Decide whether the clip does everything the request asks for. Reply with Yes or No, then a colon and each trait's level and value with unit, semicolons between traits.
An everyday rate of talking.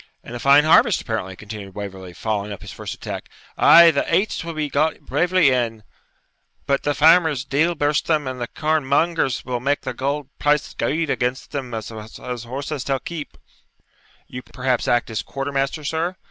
Yes: average, 180 wpm